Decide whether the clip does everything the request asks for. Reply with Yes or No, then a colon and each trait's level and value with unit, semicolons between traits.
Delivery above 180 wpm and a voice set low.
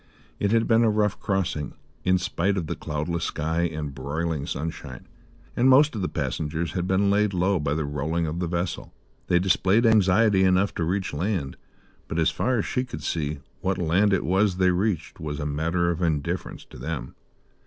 Yes: average, 195 wpm; very low, 90 Hz